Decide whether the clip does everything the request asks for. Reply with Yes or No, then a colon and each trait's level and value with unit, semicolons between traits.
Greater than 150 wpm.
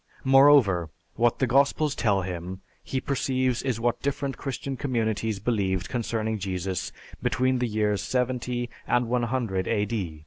No: slow, 135 wpm